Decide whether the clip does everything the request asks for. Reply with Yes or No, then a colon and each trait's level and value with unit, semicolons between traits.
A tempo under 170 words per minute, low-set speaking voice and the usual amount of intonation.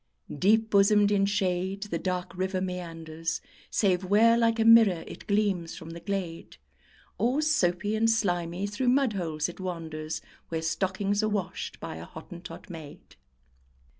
No: average, 150 wpm; high, 190 Hz; average, 3.6 semitones